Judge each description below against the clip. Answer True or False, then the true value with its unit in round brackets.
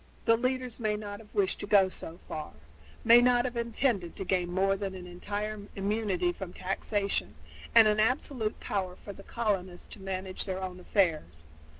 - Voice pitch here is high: True (200 Hz)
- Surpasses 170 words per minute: True (180 wpm)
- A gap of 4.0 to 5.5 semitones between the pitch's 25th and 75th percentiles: False (3.0 semitones)